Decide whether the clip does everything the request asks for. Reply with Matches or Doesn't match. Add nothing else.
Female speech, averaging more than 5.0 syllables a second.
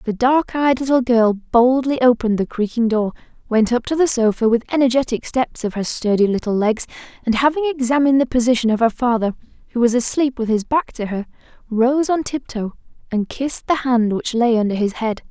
Matches